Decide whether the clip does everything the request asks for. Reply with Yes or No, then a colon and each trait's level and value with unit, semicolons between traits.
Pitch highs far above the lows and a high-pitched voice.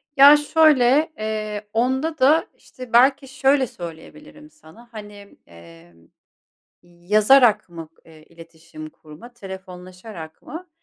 Yes: wide, 8.2 semitones; high, 215 Hz